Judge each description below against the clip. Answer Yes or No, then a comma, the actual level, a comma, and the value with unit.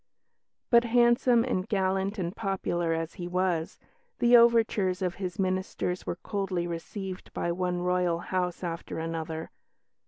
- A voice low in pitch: No, medium, 185 Hz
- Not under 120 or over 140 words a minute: Yes, slow, 135 wpm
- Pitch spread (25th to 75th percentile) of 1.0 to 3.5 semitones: Yes, narrow, 2.6 semitones